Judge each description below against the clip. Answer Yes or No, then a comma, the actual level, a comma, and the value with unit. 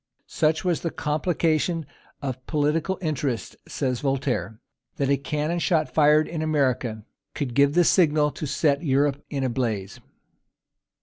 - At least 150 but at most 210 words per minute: No, average, 140 wpm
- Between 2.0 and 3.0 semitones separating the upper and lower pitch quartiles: Yes, average, 2.7 semitones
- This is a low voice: No, medium, 145 Hz